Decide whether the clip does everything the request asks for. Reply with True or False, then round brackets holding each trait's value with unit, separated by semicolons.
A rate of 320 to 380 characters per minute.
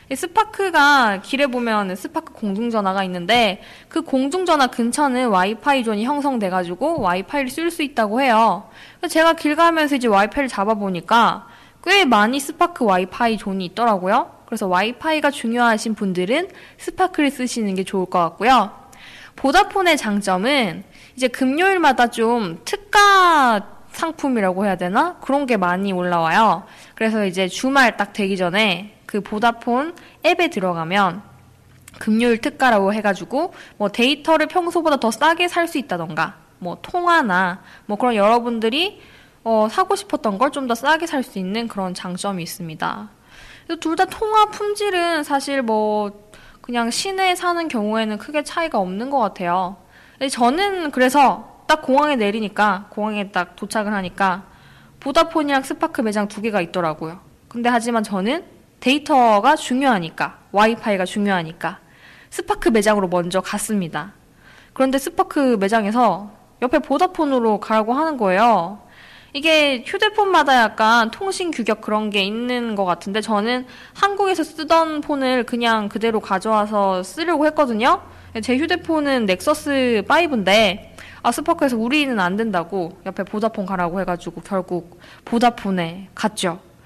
True (325 characters per minute)